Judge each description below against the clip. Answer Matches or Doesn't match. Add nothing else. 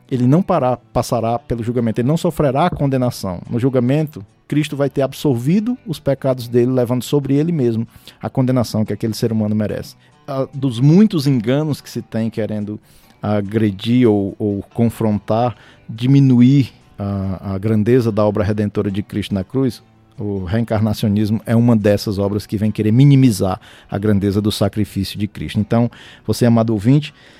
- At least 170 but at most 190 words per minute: Doesn't match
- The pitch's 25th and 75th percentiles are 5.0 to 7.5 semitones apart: Doesn't match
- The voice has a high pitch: Doesn't match